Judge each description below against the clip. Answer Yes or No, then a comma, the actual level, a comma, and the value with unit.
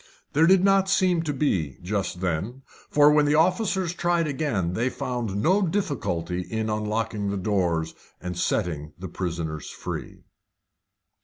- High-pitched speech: No, low, 115 Hz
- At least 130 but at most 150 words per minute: Yes, average, 145 wpm